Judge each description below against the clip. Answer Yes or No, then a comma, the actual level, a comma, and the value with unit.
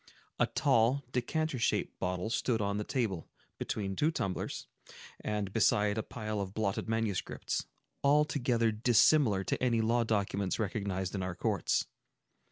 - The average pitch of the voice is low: Yes, low, 110 Hz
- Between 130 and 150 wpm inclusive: Yes, average, 140 wpm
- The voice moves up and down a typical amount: Yes, average, 3.4 semitones